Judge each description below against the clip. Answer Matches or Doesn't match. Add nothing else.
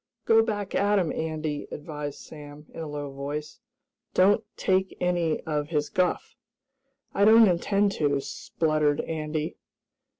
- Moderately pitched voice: Matches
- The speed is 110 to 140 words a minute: Matches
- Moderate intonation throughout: Matches